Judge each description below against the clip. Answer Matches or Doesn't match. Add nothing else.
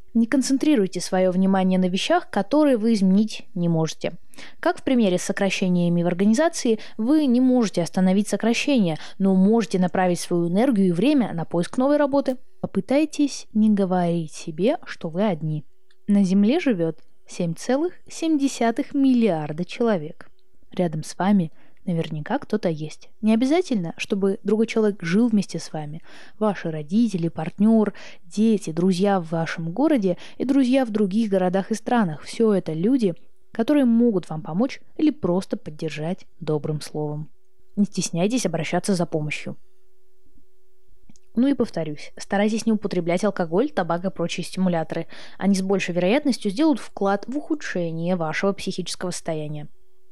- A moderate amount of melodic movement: Doesn't match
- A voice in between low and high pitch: Doesn't match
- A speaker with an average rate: Matches